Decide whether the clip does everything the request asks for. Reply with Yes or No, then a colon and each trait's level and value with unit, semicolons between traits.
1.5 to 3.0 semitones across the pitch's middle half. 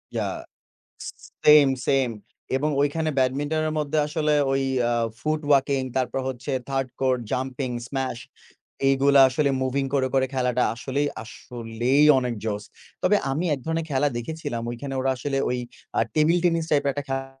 Yes: narrow, 2.5 semitones